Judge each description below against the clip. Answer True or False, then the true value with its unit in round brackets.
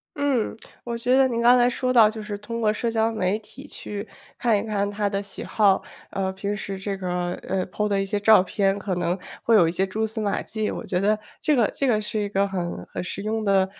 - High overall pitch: True (210 Hz)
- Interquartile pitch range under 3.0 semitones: True (2.5 semitones)